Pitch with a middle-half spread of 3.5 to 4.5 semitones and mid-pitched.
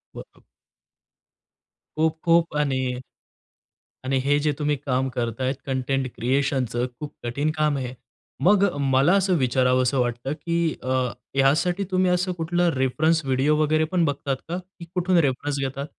Yes: average, 4.1 semitones; medium, 145 Hz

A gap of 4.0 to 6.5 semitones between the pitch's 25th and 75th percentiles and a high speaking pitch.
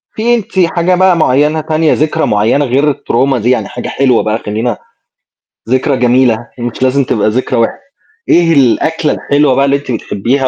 No: average, 4.3 semitones; low, 135 Hz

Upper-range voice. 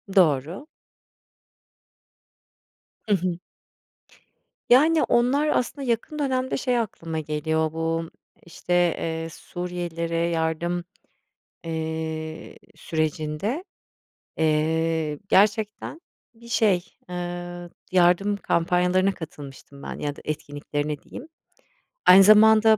No: medium, 175 Hz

